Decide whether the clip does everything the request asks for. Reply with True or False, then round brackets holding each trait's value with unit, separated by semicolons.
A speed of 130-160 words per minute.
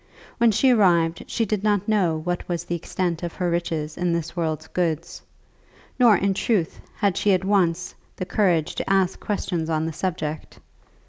False (180 wpm)